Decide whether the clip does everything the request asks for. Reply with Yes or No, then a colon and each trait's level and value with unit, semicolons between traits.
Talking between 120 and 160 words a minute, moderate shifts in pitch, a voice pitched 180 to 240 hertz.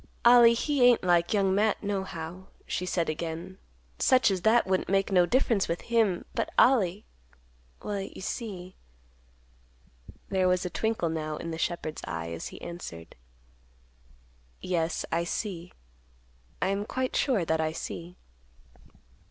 Yes: average, 140 wpm; average, 4.0 semitones; medium, 185 Hz